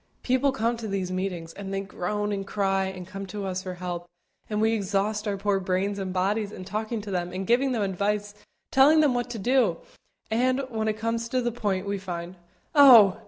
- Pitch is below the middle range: No, high, 205 Hz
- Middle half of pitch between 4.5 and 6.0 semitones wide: No, average, 3.2 semitones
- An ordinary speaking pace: No, fast, 210 wpm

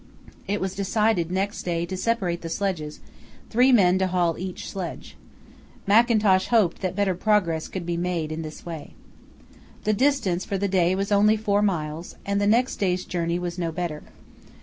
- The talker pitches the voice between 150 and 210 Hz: Yes, medium, 185 Hz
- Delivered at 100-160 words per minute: No, average, 175 wpm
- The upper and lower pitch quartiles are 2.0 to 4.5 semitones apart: Yes, average, 3.0 semitones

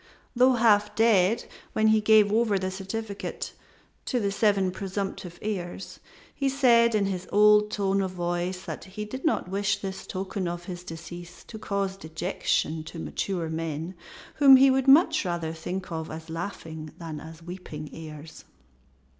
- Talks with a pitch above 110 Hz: Yes, high, 190 Hz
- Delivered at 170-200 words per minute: No, average, 160 wpm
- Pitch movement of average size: Yes, average, 3.6 semitones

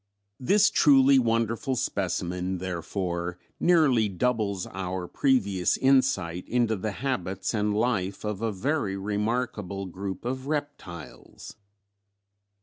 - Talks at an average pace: No, slow, 105 wpm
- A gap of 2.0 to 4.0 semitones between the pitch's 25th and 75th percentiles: No, wide, 5.4 semitones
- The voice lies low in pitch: Yes, low, 105 Hz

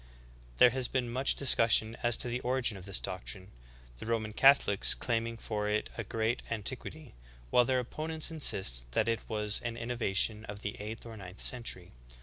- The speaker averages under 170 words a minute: No, average, 180 wpm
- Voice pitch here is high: No, low, 115 Hz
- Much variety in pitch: No, average, 2.9 semitones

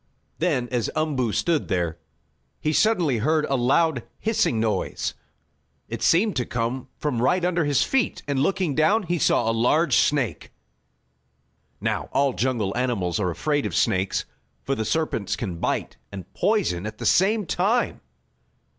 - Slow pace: No, average, 155 wpm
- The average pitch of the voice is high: No, low, 135 Hz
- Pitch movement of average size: No, wide, 6.9 semitones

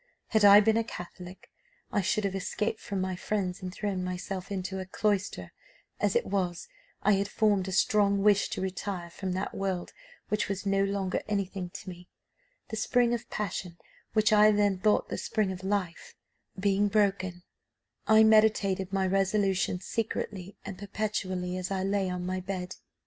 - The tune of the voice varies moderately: No, narrow, 2.0 semitones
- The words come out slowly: No, average, 170 wpm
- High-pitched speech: Yes, high, 195 Hz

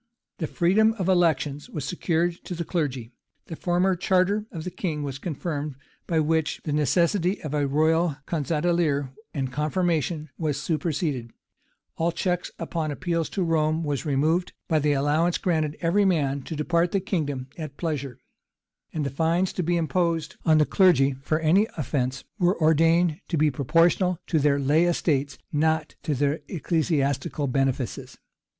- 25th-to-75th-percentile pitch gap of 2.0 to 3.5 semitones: Yes, average, 3.2 semitones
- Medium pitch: Yes, medium, 160 Hz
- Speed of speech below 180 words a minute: Yes, average, 160 wpm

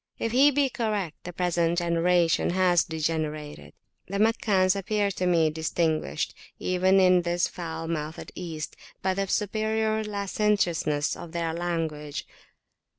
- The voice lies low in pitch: No, medium, 175 Hz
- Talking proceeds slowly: Yes, slow, 130 wpm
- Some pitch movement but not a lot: Yes, average, 3.5 semitones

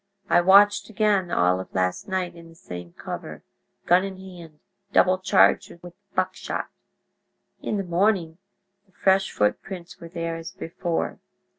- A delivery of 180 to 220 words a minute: No, average, 145 wpm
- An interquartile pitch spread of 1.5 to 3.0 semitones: Yes, narrow, 2.5 semitones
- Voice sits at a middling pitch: Yes, medium, 175 Hz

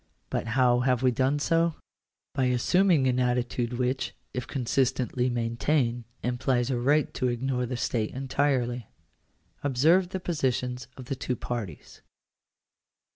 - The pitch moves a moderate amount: No, narrow, 1.9 semitones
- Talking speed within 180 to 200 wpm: No, slow, 135 wpm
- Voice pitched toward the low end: Yes, low, 125 Hz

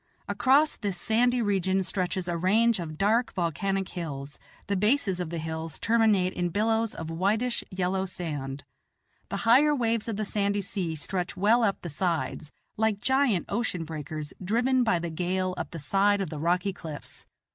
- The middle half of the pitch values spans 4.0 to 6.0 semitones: Yes, average, 4.5 semitones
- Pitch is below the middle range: No, high, 190 Hz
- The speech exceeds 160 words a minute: Yes, average, 170 wpm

